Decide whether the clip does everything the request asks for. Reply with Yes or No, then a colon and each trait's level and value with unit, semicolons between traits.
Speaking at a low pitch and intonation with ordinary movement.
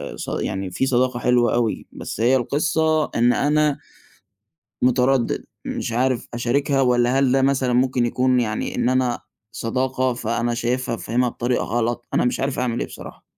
No: low, 125 Hz; narrow, 1.7 semitones